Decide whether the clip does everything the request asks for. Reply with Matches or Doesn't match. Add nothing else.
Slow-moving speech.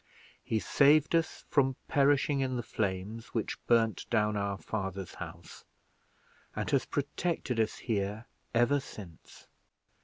Matches